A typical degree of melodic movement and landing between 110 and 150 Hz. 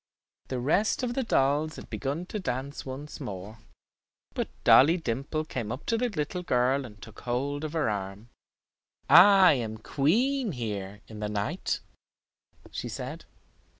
No: wide, 6.7 semitones; low, 135 Hz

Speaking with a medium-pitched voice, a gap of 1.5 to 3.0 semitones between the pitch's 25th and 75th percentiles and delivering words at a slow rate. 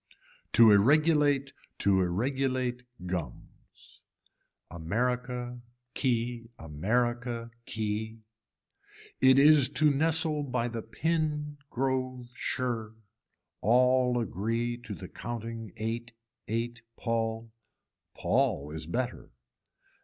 No: low, 120 Hz; narrow, 2.6 semitones; slow, 85 wpm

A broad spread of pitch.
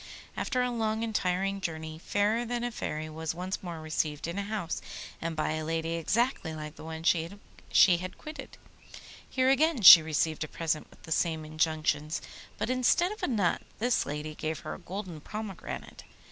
Yes: wide, 5.7 semitones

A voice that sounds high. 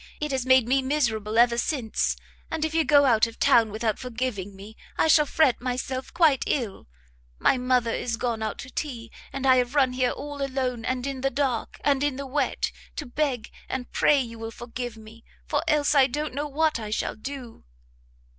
Yes: very high, 255 Hz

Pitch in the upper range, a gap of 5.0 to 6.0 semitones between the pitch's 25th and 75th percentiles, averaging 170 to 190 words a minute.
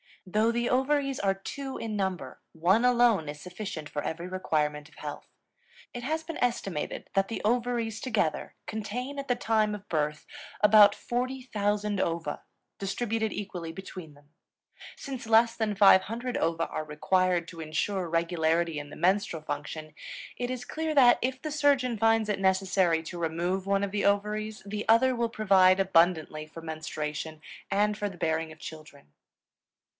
No: high, 195 Hz; wide, 5.6 semitones; average, 160 wpm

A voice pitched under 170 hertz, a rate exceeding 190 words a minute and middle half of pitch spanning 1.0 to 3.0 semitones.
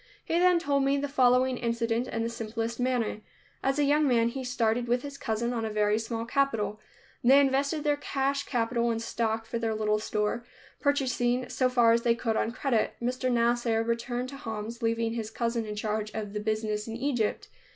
No: high, 235 Hz; average, 200 wpm; narrow, 2.5 semitones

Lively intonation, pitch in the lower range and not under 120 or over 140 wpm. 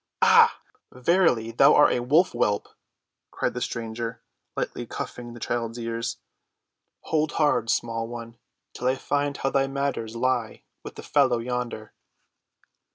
No: average, 2.9 semitones; low, 120 Hz; slow, 135 wpm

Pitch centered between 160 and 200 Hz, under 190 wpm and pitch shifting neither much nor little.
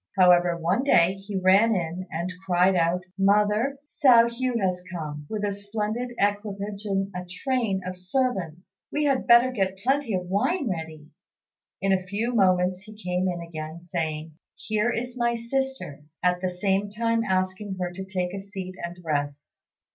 Yes: high, 190 Hz; average, 170 wpm; average, 3.9 semitones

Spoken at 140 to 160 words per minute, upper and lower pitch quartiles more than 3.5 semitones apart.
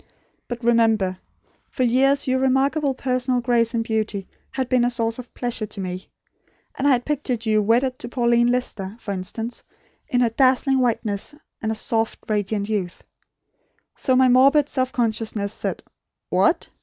No: average, 155 wpm; average, 2.9 semitones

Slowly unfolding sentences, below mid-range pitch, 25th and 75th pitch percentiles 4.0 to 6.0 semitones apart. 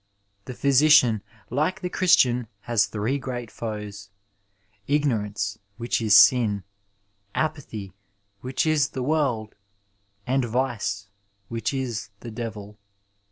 Yes: slow, 115 wpm; low, 120 Hz; average, 4.3 semitones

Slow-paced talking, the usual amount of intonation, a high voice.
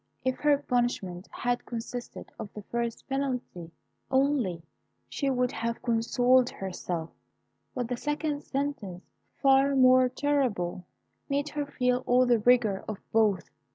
Yes: slow, 130 wpm; average, 3.8 semitones; high, 245 Hz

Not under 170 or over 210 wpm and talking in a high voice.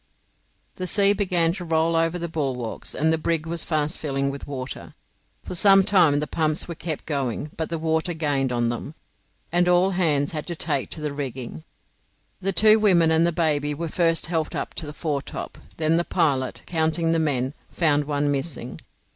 No: average, 190 wpm; medium, 160 Hz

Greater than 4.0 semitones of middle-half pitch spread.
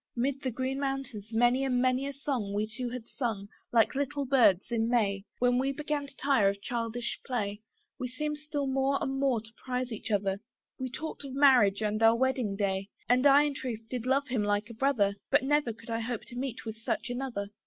No: average, 3.6 semitones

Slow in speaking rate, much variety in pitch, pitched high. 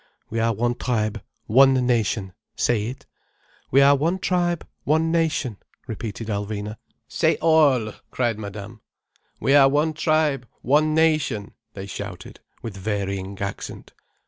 No: slow, 125 wpm; wide, 6.0 semitones; low, 120 Hz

